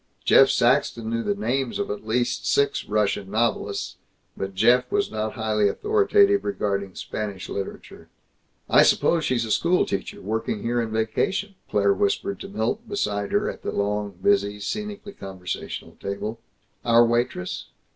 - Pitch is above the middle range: No, low, 110 Hz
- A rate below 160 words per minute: Yes, average, 150 wpm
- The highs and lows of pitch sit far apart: No, average, 4.7 semitones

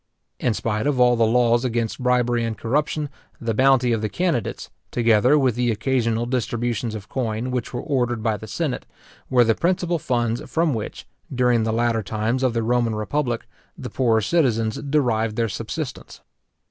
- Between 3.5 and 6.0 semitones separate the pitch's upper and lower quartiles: No, narrow, 2.5 semitones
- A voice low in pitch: Yes, low, 120 Hz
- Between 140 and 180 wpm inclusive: Yes, average, 170 wpm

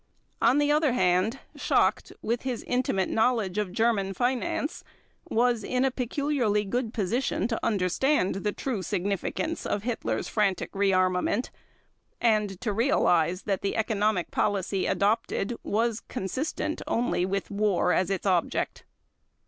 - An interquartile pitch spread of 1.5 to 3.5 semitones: No, average, 4.2 semitones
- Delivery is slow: Yes, slow, 130 wpm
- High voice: Yes, high, 215 Hz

